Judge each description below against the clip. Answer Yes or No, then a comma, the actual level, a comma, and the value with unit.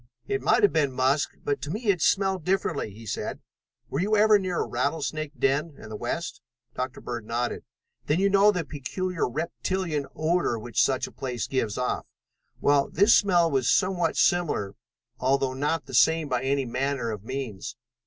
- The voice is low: No, medium, 145 Hz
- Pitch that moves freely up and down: Yes, wide, 5.7 semitones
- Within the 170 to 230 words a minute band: Yes, average, 180 wpm